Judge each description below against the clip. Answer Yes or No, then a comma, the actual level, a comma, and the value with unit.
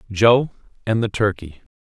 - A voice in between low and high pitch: No, low, 105 Hz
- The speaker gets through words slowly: Yes, slow, 130 wpm